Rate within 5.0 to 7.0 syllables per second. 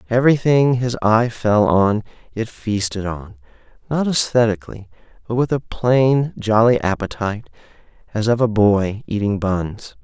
No: 4.5 syllables/s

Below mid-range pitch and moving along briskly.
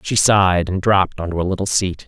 Yes: very low, 95 Hz; fast, 230 wpm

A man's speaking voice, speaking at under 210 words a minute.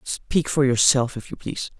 Yes: male; average, 200 wpm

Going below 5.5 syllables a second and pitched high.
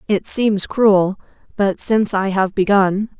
Yes: 3.9 syllables/s; high, 200 Hz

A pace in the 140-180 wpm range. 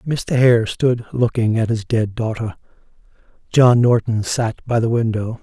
Yes: average, 155 wpm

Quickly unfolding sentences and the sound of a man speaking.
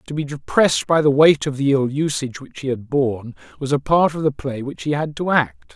Yes: fast, 260 wpm; male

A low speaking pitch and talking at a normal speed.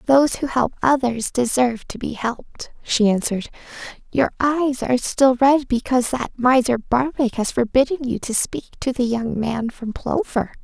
No: very high, 250 Hz; average, 170 wpm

